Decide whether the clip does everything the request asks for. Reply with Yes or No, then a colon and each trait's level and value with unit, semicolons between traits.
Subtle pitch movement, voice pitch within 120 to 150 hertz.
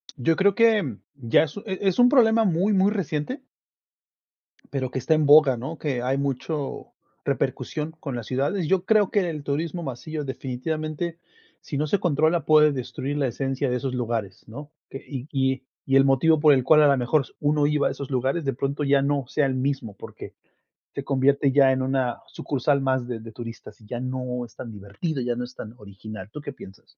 No: average, 3.5 semitones; medium, 140 Hz